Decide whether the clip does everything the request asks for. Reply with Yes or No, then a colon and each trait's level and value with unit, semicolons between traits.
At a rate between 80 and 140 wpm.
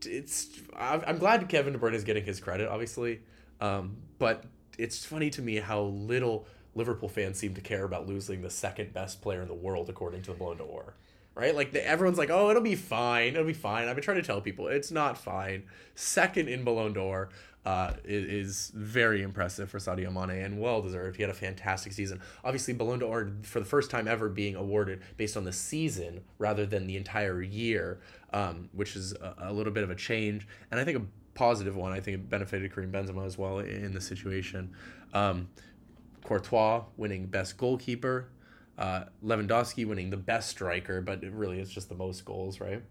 No: average, 200 wpm